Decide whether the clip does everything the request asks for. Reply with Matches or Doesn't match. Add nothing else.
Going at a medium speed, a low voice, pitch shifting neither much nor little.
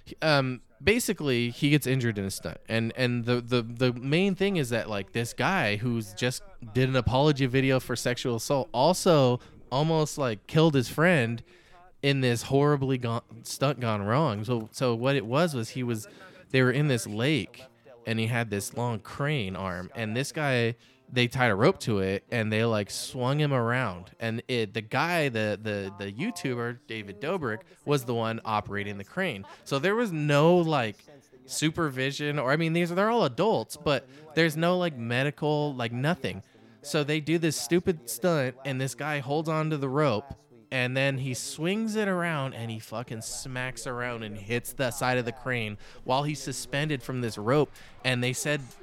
Matches